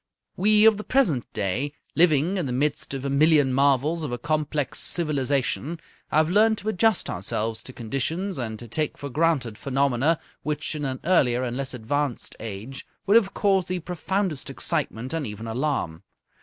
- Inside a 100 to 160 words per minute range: No, average, 170 wpm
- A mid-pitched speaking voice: Yes, medium, 145 Hz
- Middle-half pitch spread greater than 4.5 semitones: Yes, average, 5.1 semitones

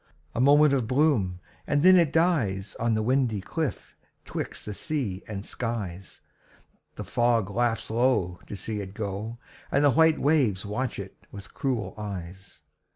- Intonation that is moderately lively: No, wide, 5.8 semitones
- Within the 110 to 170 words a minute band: Yes, average, 155 wpm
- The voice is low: Yes, low, 115 Hz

